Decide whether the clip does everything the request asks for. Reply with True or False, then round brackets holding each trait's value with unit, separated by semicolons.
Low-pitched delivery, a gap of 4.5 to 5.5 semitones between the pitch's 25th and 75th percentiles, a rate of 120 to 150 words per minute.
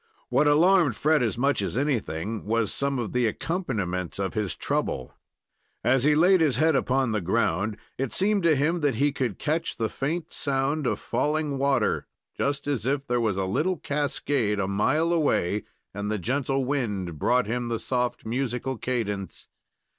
False (130 Hz; 5.2 semitones; 175 wpm)